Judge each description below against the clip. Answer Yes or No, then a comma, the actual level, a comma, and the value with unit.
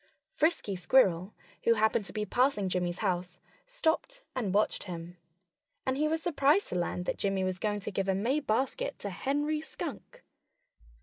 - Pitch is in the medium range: No, high, 215 Hz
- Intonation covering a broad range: Yes, wide, 7.9 semitones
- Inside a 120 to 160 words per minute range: No, average, 170 wpm